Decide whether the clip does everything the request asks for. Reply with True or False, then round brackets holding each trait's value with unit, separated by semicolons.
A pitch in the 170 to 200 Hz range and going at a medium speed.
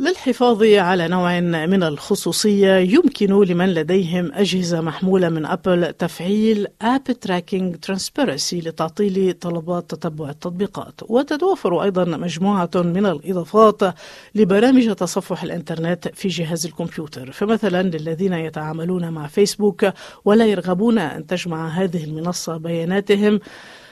True (185 Hz; 110 wpm)